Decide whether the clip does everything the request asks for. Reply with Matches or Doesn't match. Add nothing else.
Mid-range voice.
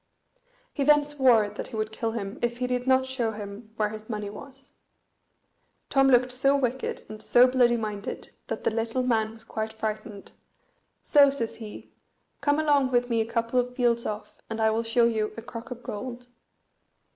Doesn't match